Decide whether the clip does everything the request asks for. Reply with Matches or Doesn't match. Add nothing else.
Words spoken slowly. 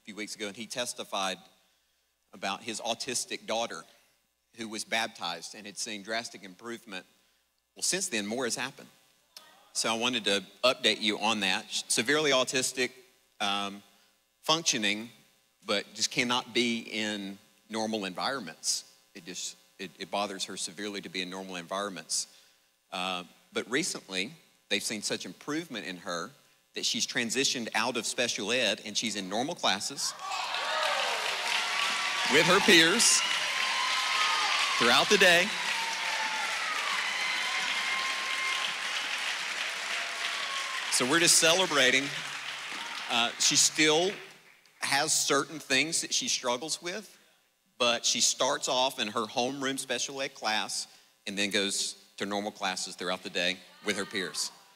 Matches